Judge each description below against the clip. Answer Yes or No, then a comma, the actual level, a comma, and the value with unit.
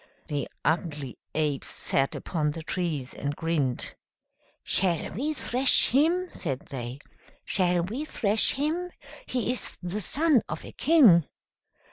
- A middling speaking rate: No, slow, 130 wpm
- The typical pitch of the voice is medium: Yes, medium, 175 Hz